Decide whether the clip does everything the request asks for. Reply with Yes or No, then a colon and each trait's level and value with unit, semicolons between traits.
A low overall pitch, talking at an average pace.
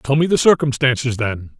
Yes: low, 130 Hz; average, 190 wpm